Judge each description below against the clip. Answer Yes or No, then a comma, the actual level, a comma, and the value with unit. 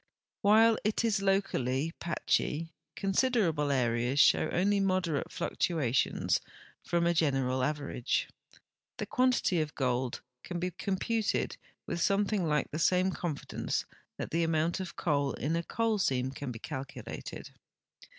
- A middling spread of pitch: No, wide, 5.7 semitones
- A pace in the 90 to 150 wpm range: Yes, average, 140 wpm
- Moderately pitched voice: Yes, medium, 165 Hz